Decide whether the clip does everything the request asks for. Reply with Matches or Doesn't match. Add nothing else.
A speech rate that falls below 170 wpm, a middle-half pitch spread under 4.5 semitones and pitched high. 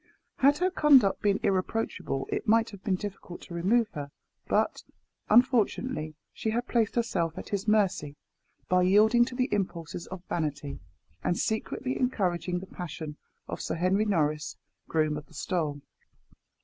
Doesn't match